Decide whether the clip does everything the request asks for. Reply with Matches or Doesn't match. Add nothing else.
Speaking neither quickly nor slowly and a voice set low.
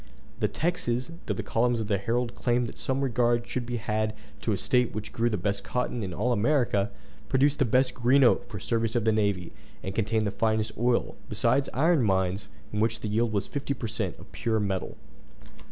Doesn't match